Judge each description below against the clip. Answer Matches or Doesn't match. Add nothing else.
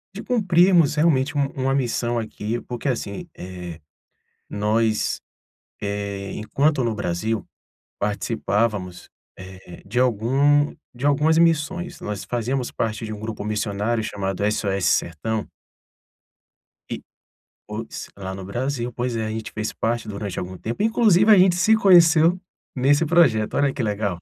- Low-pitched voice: Matches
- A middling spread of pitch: Doesn't match